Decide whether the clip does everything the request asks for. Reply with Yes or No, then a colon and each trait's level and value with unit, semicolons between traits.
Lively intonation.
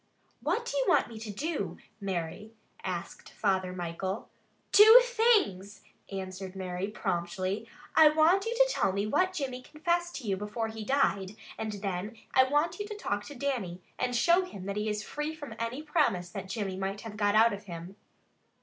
Yes: wide, 7.6 semitones